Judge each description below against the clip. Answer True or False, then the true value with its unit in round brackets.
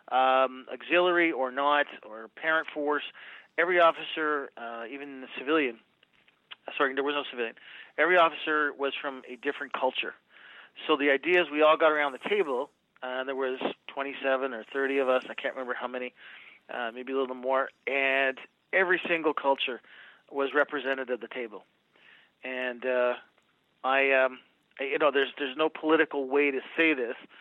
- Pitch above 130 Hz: True (140 Hz)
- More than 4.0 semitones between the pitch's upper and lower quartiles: False (2.9 semitones)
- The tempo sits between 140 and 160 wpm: False (175 wpm)